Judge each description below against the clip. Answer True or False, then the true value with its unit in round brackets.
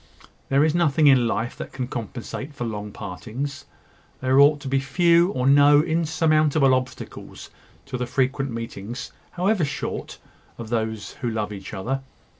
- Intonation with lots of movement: False (4.0 semitones)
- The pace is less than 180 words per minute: True (155 wpm)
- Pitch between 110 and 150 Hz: True (135 Hz)